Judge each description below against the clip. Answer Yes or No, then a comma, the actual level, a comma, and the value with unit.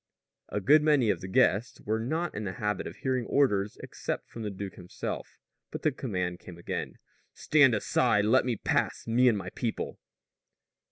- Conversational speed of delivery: Yes, average, 180 wpm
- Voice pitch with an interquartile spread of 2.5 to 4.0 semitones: No, average, 4.6 semitones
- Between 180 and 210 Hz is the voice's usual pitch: No, low, 110 Hz